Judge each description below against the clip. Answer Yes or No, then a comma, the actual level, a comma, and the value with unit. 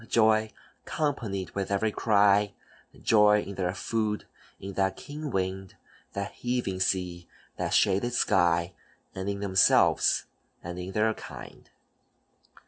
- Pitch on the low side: Yes, low, 100 Hz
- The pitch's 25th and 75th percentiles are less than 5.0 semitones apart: Yes, narrow, 2.6 semitones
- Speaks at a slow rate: Yes, slow, 125 wpm